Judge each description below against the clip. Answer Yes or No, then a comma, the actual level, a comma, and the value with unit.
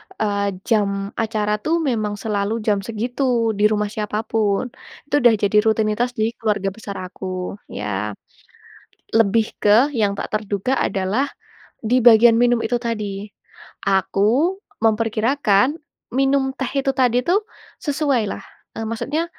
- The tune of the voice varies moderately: Yes, average, 3.2 semitones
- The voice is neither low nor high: No, high, 220 Hz